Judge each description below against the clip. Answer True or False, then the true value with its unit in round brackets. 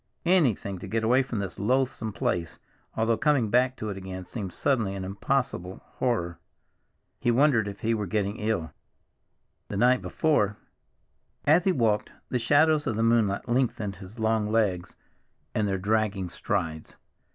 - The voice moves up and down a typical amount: True (4.1 semitones)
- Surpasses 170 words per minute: False (155 wpm)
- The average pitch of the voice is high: False (110 Hz)